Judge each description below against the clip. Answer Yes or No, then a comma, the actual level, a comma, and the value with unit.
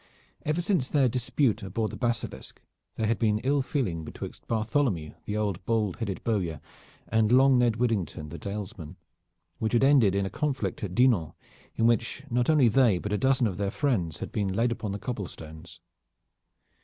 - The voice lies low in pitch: Yes, low, 110 Hz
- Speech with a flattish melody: No, average, 4.5 semitones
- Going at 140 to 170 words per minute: No, average, 180 wpm